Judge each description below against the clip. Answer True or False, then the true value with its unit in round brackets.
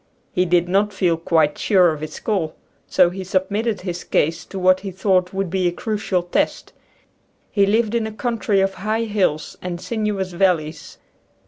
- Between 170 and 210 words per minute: True (180 wpm)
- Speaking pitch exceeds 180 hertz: True (190 Hz)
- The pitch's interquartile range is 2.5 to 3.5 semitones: True (3.0 semitones)